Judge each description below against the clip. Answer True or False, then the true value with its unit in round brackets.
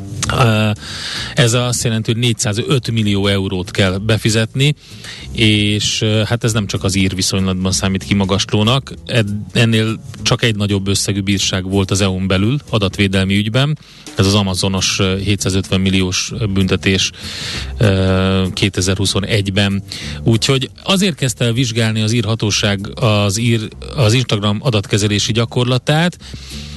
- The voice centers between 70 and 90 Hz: False (105 Hz)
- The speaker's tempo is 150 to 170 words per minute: False (115 wpm)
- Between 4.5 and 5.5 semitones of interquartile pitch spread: False (3.3 semitones)